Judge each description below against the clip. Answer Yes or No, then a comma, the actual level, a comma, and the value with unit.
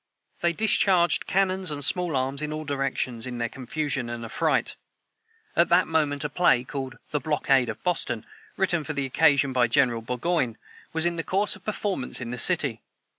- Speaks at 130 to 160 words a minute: No, average, 180 wpm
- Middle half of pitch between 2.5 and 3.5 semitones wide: No, average, 5.2 semitones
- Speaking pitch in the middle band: Yes, medium, 145 Hz